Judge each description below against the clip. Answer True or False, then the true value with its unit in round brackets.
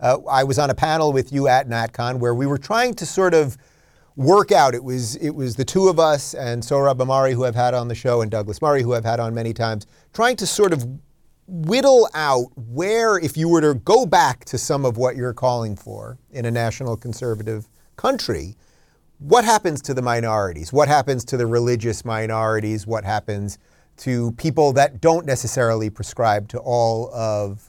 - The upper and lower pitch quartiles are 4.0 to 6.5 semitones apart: True (4.7 semitones)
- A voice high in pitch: False (125 Hz)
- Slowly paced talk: False (200 wpm)